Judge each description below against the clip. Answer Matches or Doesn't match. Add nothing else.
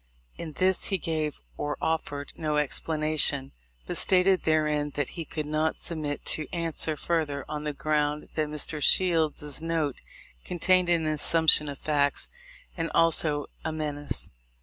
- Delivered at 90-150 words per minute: Matches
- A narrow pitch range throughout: Matches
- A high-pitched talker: Doesn't match